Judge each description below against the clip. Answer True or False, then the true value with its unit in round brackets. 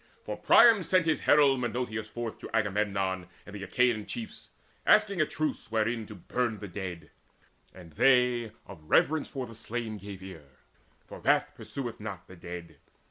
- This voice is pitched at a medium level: False (110 Hz)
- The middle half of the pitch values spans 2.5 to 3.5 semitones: False (4.6 semitones)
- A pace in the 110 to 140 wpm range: False (165 wpm)